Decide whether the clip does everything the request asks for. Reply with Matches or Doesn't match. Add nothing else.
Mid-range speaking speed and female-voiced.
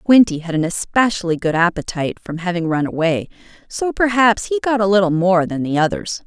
Matches